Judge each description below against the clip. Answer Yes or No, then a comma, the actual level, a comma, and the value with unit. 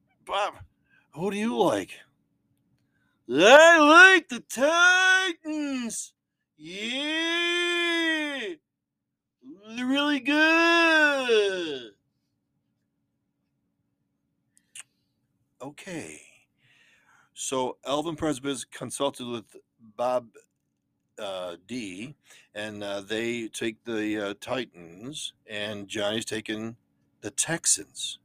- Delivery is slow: Yes, slow, 75 wpm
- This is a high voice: No, medium, 150 Hz